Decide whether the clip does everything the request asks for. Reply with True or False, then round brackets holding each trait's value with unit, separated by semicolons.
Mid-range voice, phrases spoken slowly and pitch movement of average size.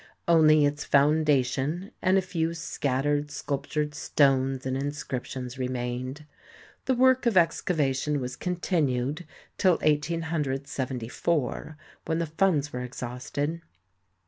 True (145 Hz; 110 wpm; 3.8 semitones)